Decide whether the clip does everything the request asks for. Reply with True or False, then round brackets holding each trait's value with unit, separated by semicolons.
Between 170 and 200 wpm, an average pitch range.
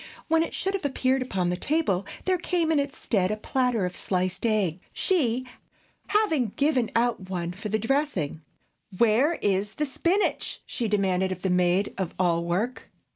False (175 wpm; 7.3 semitones)